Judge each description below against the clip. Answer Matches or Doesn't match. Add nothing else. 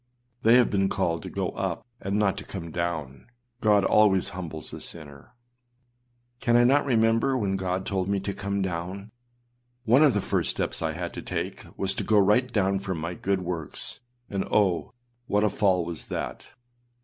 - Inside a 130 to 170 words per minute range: Doesn't match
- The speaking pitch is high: Doesn't match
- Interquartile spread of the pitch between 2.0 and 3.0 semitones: Doesn't match